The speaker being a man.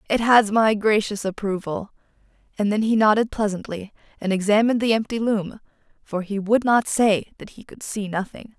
No: female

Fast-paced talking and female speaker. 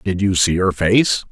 No: fast, 230 wpm; male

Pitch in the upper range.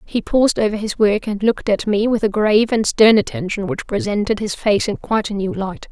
Yes: high, 205 Hz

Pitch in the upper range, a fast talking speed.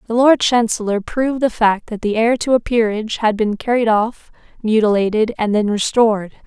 No: high, 225 Hz; average, 185 wpm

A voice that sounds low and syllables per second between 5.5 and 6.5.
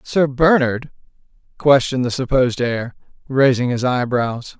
No: low, 130 Hz; 4.6 syllables/s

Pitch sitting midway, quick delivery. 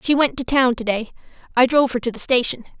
No: very high, 250 Hz; fast, 215 wpm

